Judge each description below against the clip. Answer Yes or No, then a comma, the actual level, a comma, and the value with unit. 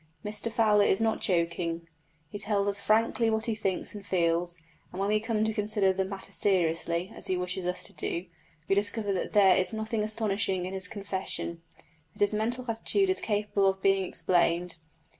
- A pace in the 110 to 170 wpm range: No, average, 190 wpm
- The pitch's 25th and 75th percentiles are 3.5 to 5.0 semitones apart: No, average, 2.8 semitones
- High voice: Yes, high, 200 Hz